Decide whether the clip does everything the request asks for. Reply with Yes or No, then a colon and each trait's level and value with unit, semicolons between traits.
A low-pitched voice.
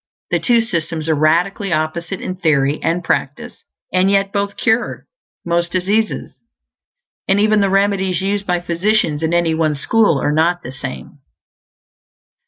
No: medium, 175 Hz